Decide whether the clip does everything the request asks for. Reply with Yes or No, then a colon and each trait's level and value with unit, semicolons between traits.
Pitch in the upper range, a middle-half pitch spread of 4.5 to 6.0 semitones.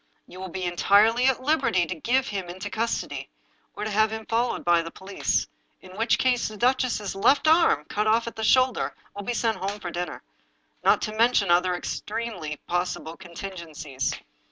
Yes: high, 205 Hz; average, 4.8 semitones